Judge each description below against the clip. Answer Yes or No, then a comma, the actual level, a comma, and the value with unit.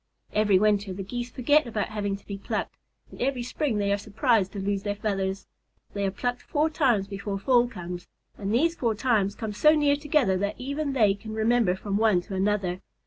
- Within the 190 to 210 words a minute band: Yes, fast, 205 wpm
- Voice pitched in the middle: No, high, 210 Hz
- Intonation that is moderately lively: Yes, average, 3.8 semitones